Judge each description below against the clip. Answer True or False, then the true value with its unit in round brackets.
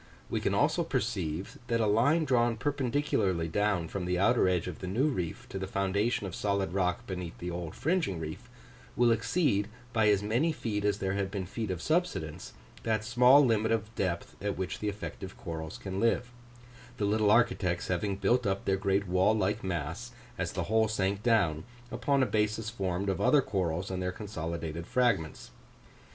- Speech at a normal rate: True (185 wpm)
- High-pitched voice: False (100 Hz)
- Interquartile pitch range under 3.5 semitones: False (3.9 semitones)